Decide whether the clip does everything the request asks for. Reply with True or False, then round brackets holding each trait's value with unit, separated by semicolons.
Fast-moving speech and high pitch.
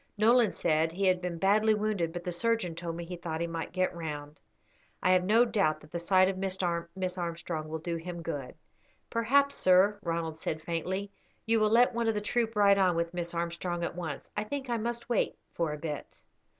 False (215 wpm; 180 Hz)